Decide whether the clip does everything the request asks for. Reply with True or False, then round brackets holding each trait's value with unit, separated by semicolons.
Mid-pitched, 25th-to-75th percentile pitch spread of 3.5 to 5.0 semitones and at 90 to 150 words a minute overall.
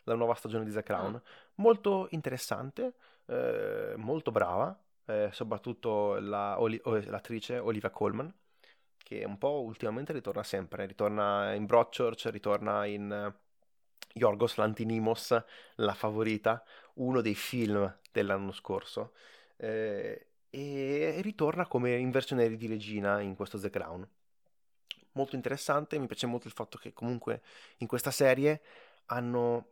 False (115 Hz; 4.3 semitones; 130 wpm)